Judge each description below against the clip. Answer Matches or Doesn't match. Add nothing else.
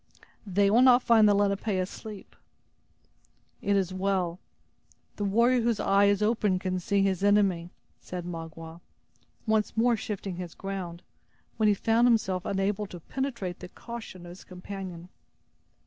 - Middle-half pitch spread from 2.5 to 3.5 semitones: Matches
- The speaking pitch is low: Doesn't match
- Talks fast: Doesn't match